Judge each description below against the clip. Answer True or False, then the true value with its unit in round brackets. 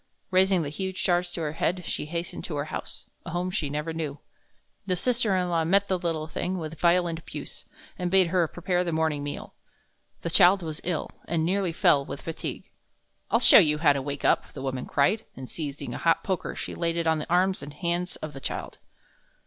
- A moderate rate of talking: False (215 wpm)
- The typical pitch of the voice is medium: True (170 Hz)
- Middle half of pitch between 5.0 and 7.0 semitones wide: False (2.9 semitones)